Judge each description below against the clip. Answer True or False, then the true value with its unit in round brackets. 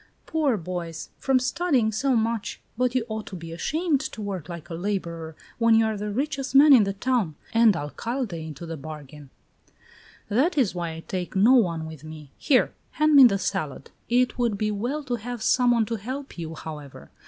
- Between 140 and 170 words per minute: False (200 wpm)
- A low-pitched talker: False (215 Hz)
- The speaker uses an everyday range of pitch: False (7.2 semitones)